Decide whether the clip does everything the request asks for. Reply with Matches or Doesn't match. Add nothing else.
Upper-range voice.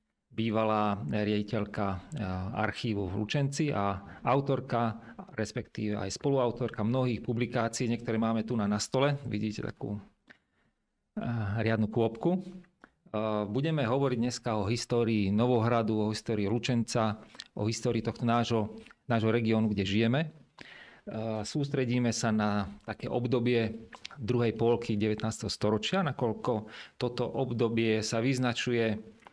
Doesn't match